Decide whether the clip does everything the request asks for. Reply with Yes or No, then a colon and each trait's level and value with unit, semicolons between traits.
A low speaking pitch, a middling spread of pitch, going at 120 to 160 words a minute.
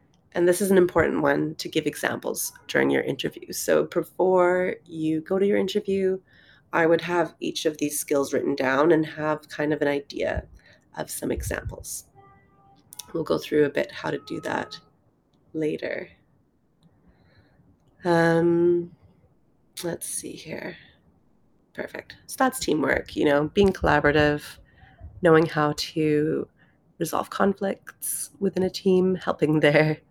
No: medium, 160 Hz; average, 3.3 semitones; average, 140 wpm